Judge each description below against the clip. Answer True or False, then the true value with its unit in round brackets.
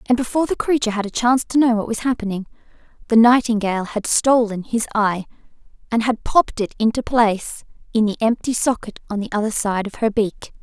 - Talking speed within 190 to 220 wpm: True (200 wpm)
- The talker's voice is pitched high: True (225 Hz)